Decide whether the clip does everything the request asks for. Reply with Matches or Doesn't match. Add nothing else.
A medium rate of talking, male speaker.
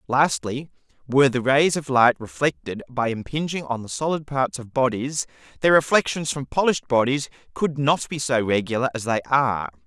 Matches